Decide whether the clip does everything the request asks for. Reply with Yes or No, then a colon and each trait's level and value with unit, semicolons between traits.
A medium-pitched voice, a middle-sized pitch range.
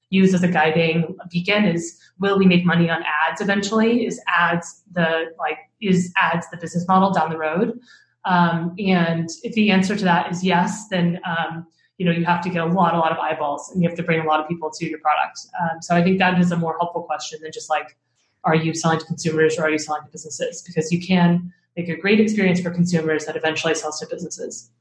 No: medium, 170 Hz; narrow, 2.3 semitones